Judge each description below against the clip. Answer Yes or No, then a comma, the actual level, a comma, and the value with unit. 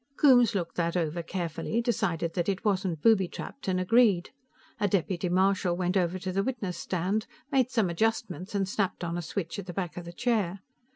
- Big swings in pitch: No, average, 3.2 semitones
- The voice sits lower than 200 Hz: Yes, medium, 185 Hz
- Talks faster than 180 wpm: Yes, average, 195 wpm